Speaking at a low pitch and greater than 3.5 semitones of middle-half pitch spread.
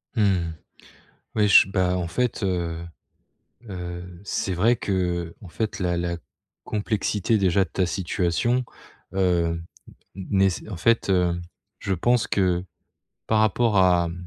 No: very low, 95 Hz; average, 2.9 semitones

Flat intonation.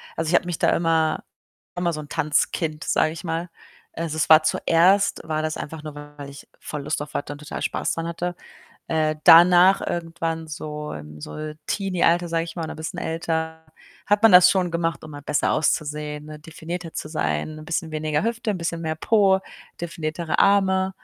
Yes: narrow, 2.2 semitones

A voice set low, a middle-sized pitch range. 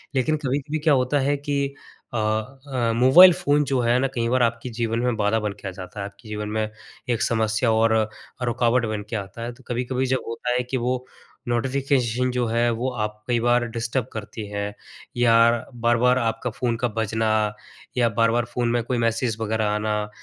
No: low, 120 Hz; narrow, 2.3 semitones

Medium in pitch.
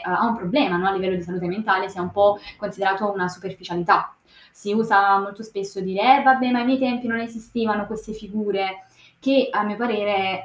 No: high, 205 Hz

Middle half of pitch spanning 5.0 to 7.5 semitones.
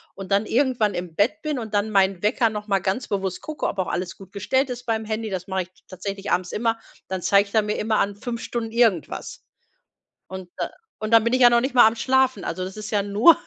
No: average, 3.4 semitones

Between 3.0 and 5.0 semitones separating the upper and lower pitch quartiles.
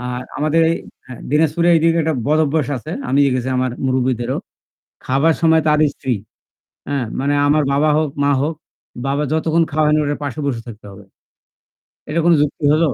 Yes: average, 3.3 semitones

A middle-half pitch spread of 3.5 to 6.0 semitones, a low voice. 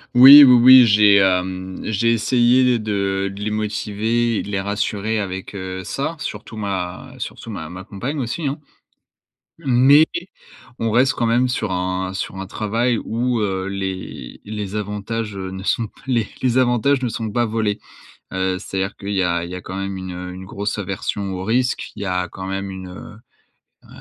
Yes: average, 3.8 semitones; low, 105 Hz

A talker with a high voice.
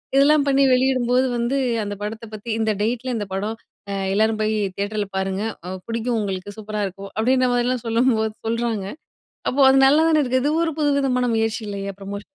Yes: high, 225 Hz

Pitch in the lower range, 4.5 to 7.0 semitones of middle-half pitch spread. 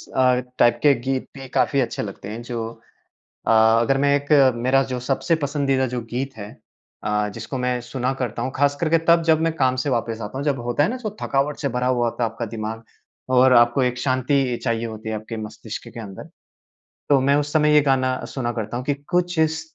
No: low, 130 Hz; average, 3.3 semitones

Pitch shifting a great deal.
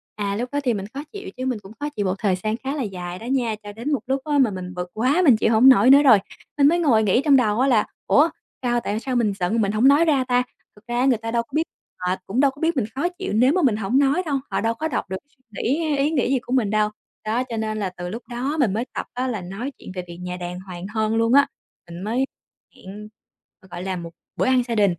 No: average, 4.7 semitones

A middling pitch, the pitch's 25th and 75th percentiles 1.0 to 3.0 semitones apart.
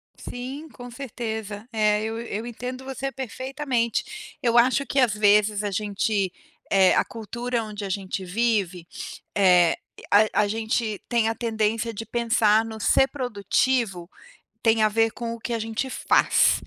No: high, 225 Hz; narrow, 2.6 semitones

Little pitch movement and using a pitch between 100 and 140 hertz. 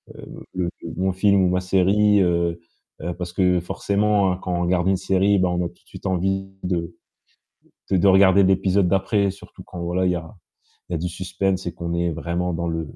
No: narrow, 1.7 semitones; very low, 90 Hz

